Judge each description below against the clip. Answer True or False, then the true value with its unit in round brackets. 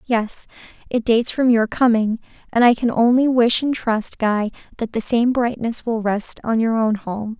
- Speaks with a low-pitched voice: False (230 Hz)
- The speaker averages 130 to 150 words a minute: False (195 wpm)